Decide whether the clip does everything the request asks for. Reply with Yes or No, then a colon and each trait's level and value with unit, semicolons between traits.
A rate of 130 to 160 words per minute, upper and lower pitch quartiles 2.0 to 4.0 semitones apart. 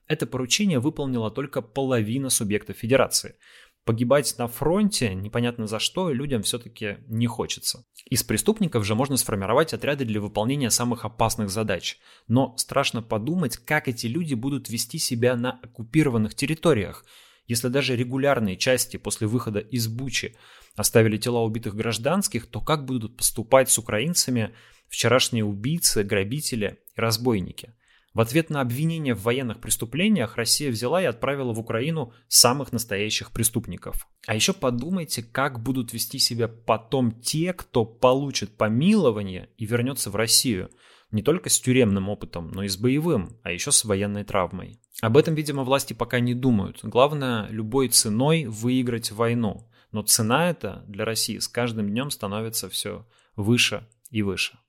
Yes: average, 145 wpm; average, 3.5 semitones